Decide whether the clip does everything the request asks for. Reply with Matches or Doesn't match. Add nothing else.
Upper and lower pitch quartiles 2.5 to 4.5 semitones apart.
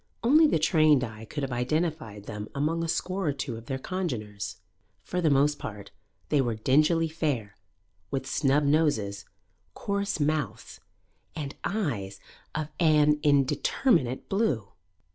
Doesn't match